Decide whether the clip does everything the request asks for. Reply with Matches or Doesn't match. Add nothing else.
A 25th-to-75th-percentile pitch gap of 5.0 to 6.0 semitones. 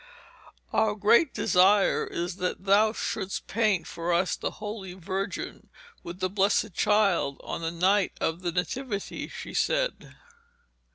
Doesn't match